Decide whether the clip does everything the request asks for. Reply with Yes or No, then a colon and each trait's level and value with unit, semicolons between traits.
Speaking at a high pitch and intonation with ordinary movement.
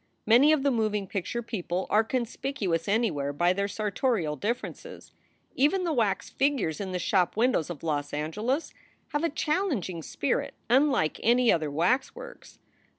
No: high, 215 Hz; wide, 7.3 semitones